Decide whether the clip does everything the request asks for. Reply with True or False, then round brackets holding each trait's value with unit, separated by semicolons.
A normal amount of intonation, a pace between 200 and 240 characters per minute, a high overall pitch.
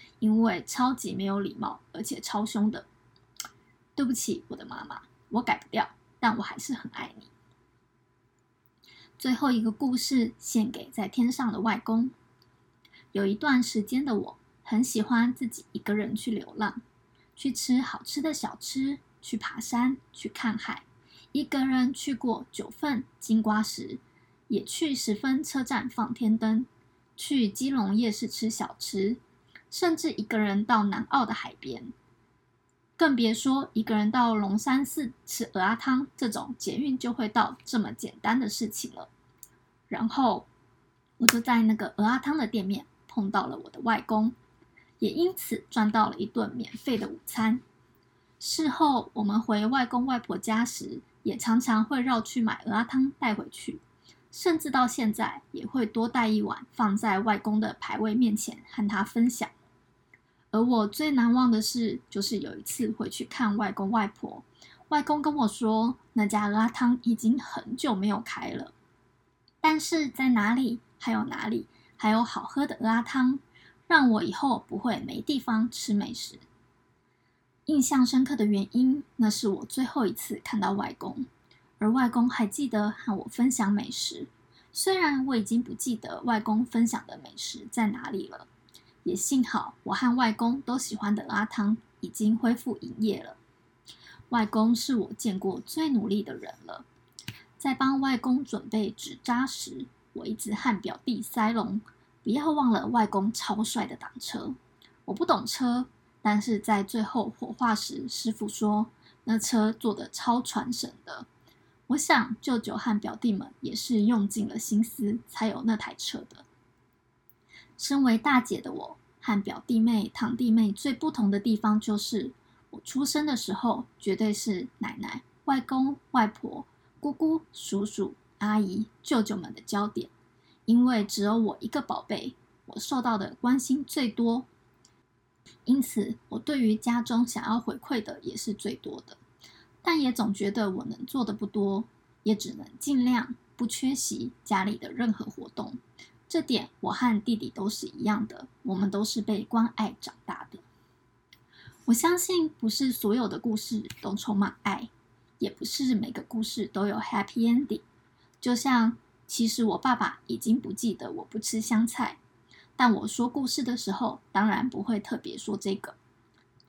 True (3.2 semitones; 230 characters per minute; 230 Hz)